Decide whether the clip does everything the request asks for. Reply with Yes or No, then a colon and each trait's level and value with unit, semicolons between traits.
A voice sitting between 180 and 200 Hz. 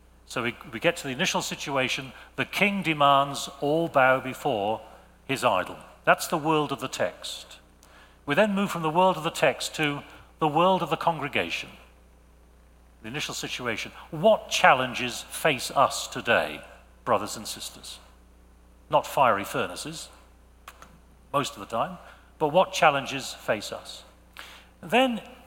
No: medium, 140 Hz